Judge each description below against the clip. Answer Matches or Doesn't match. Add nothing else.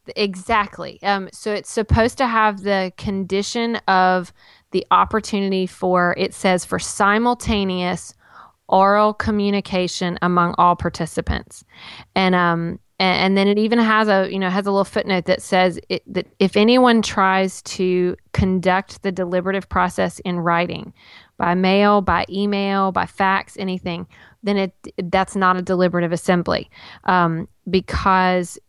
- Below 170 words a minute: Matches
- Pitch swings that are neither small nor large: Doesn't match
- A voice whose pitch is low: Doesn't match